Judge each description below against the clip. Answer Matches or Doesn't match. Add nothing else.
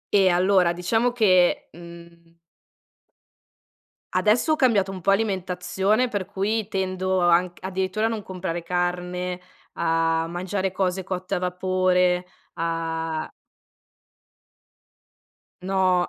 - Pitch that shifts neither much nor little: Doesn't match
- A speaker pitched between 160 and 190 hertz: Matches